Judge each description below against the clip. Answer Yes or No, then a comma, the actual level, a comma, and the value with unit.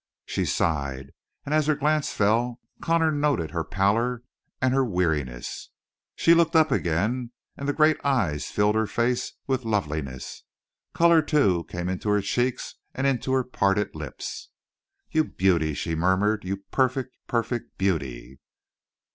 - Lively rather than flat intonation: Yes, wide, 7.6 semitones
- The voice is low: Yes, low, 110 Hz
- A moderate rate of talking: Yes, average, 145 wpm